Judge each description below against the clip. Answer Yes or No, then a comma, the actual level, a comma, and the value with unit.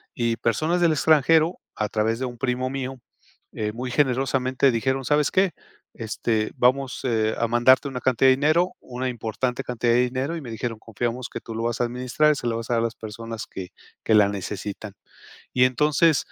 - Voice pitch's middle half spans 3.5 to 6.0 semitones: No, average, 2.8 semitones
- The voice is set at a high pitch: No, low, 125 Hz